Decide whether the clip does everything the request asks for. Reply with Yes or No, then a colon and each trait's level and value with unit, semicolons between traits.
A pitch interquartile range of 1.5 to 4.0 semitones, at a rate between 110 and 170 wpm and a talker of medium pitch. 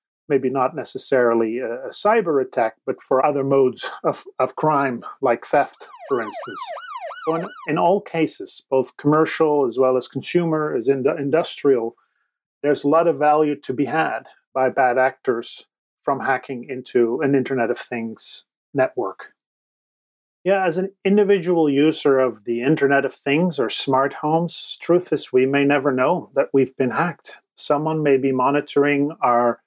Yes: average, 3.5 semitones; average, 160 wpm; medium, 145 Hz